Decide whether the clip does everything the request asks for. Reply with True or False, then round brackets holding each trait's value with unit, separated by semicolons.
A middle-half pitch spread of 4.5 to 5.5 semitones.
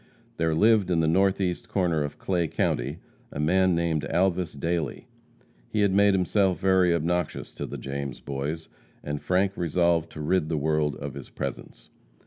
False (3.6 semitones)